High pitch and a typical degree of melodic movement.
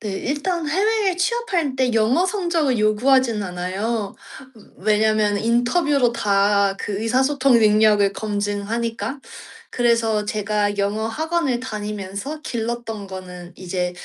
Yes: high, 225 Hz; average, 4.7 semitones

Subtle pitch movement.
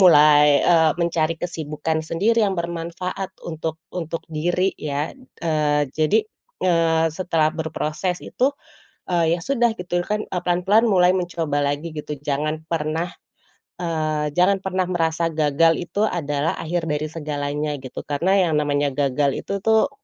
No: average, 3.0 semitones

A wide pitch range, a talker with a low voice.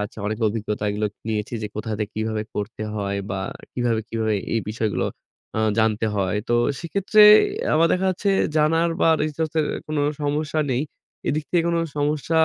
Yes: wide, 6.5 semitones; low, 115 Hz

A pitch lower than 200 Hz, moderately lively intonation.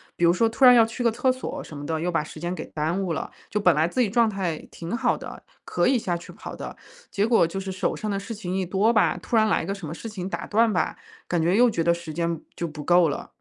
Yes: high, 190 Hz; average, 4.7 semitones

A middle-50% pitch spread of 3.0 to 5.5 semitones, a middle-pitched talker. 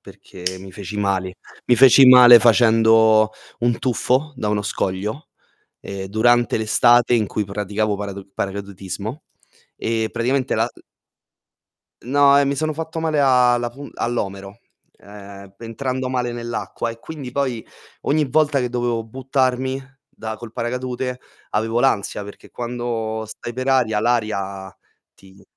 No: average, 3.6 semitones; low, 120 Hz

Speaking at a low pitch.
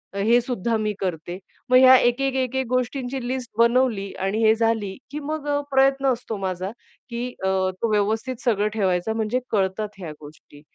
No: high, 225 Hz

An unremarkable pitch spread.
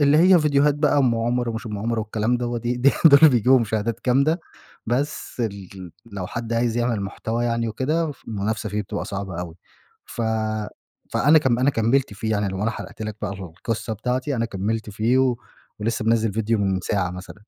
Yes: average, 3.3 semitones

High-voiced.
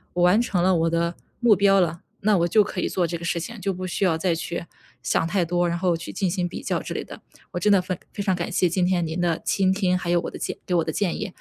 No: medium, 180 Hz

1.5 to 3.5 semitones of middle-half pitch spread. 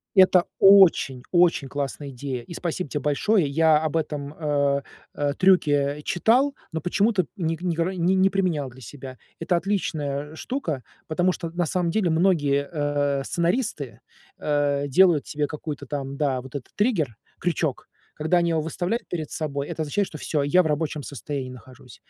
No: average, 3.9 semitones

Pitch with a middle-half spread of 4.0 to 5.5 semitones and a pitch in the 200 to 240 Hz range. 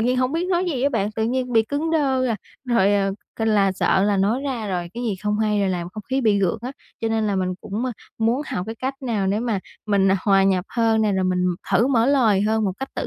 Yes: average, 4.3 semitones; high, 220 Hz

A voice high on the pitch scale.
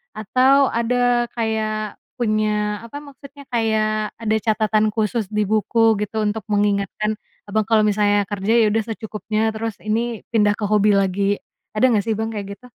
Yes: high, 215 Hz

